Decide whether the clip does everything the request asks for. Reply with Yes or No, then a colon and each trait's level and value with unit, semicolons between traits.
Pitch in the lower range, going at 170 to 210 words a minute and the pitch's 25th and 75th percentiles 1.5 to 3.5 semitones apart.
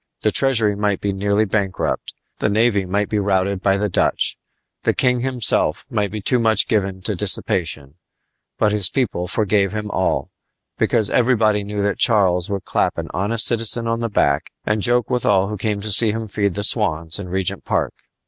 Yes: low, 105 Hz; average, 190 wpm; narrow, 2.5 semitones